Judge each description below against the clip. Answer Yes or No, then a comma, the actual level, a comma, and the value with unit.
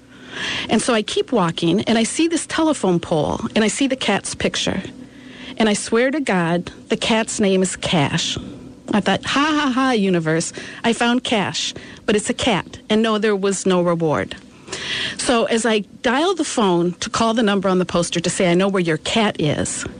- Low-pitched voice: No, high, 215 Hz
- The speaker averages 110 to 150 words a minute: No, average, 200 wpm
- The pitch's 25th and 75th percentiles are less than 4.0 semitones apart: No, average, 5.1 semitones